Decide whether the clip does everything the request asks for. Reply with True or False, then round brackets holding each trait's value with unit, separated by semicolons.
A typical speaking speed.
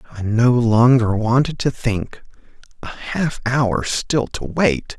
True (145 wpm)